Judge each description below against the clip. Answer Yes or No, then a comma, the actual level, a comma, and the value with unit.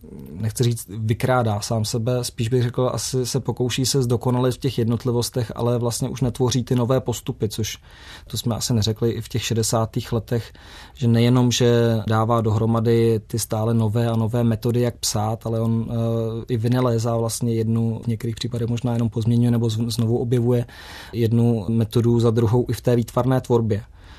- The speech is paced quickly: Yes, fast, 180 wpm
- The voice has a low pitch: Yes, low, 115 Hz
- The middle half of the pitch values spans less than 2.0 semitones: Yes, narrow, 1.3 semitones